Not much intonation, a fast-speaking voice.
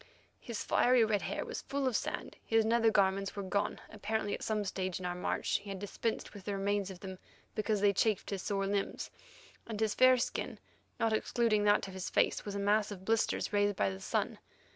Yes: narrow, 2.0 semitones; fast, 215 wpm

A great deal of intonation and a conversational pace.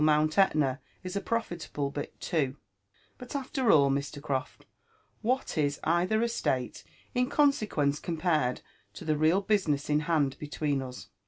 Yes: wide, 5.9 semitones; average, 145 wpm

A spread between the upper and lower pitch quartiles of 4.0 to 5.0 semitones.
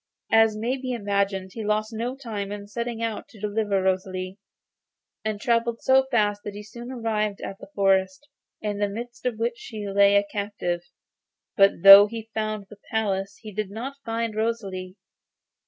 No: narrow, 2.4 semitones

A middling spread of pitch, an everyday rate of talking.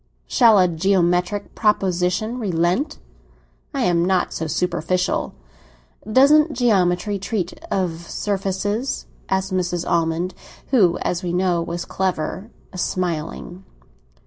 No: average, 3.0 semitones; slow, 105 wpm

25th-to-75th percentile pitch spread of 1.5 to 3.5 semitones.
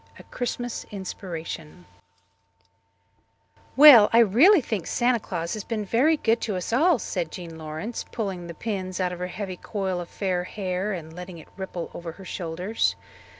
No: average, 4.4 semitones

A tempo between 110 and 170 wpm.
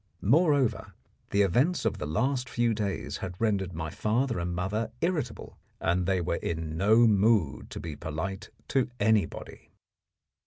Yes: average, 150 wpm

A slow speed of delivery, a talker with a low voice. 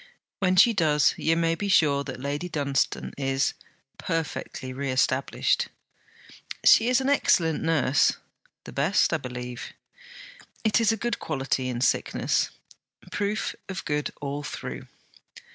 No: slow, 130 wpm; medium, 155 Hz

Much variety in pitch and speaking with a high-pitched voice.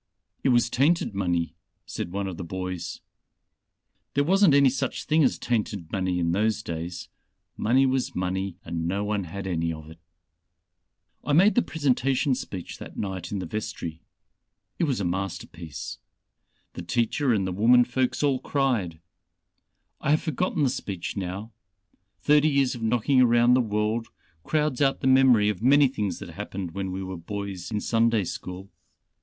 No: wide, 6.2 semitones; low, 105 Hz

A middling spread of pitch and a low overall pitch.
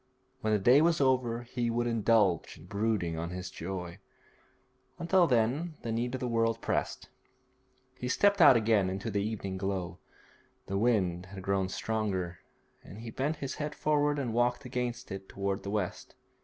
Yes: average, 4.4 semitones; low, 115 Hz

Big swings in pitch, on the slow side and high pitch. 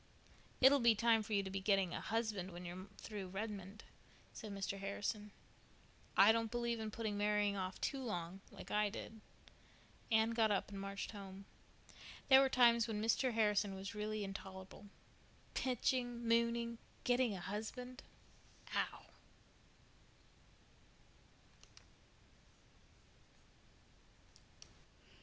No: average, 2.8 semitones; slow, 120 wpm; high, 210 Hz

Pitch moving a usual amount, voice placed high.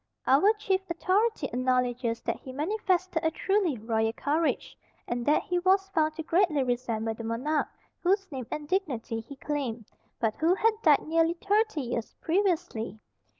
No: wide, 7.3 semitones; very high, 305 Hz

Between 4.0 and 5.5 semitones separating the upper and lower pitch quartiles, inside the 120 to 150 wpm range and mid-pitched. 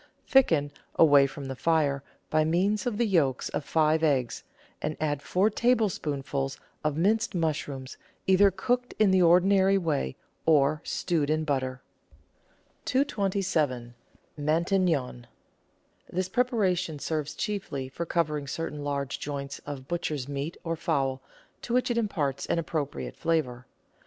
Yes: average, 5.1 semitones; slow, 135 wpm; medium, 155 Hz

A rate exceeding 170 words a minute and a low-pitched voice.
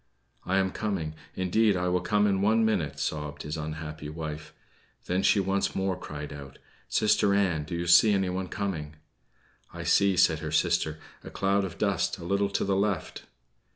Yes: average, 180 wpm; very low, 90 Hz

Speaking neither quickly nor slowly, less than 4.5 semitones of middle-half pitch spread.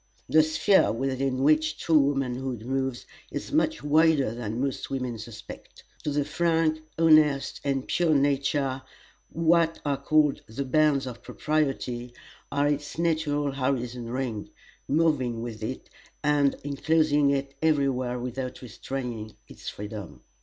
No: slow, 130 wpm; average, 3.4 semitones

